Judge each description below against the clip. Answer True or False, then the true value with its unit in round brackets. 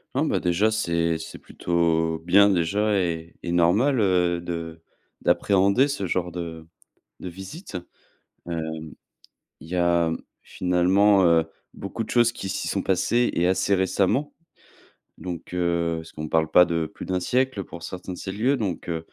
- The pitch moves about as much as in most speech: True (3.0 semitones)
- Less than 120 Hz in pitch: True (90 Hz)